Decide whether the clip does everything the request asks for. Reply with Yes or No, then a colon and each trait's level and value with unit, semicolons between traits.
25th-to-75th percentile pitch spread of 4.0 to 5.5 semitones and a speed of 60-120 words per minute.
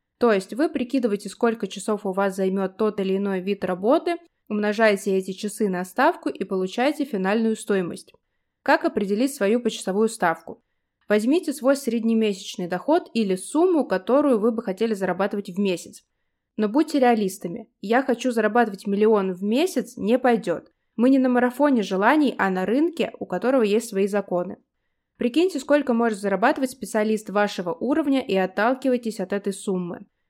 No: average, 4.3 semitones; average, 150 wpm